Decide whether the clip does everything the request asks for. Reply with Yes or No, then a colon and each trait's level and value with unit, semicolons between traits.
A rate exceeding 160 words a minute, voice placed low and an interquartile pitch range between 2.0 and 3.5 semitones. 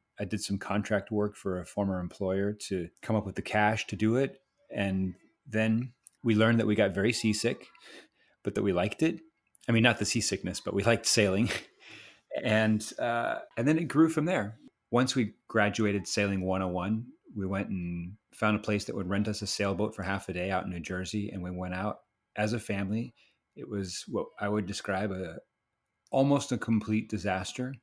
Yes: fast, 205 wpm; low, 105 Hz; average, 2.7 semitones